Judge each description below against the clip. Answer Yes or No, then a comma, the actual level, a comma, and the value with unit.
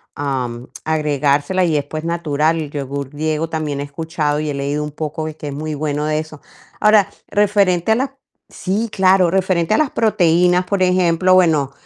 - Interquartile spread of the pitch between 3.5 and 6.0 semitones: Yes, average, 3.9 semitones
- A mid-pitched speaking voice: Yes, medium, 155 Hz